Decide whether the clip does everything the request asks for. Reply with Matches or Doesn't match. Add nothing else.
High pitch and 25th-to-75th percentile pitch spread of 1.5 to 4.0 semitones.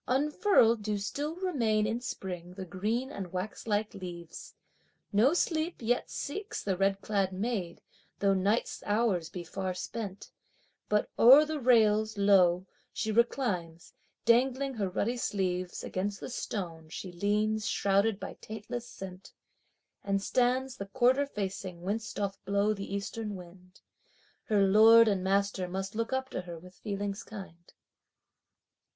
Matches